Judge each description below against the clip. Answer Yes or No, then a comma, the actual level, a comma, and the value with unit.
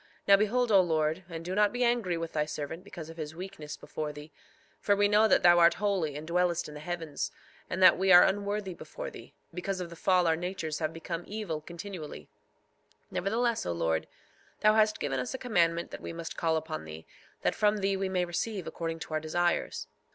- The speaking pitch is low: No, medium, 175 Hz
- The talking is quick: Yes, fast, 215 wpm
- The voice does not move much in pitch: No, average, 3.9 semitones